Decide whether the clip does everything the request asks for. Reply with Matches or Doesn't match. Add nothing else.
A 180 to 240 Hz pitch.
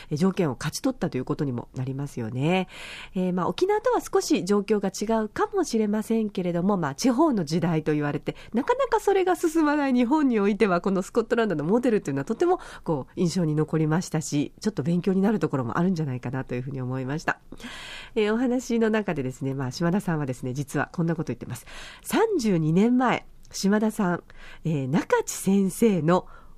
Matches